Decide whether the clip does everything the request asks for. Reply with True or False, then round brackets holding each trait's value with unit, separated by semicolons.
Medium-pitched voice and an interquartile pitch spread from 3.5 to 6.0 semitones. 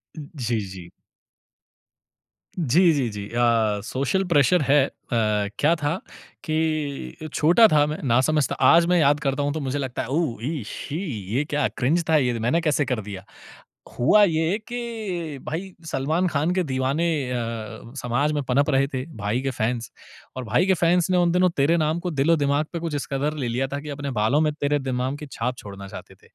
True (145 Hz; 4.3 semitones)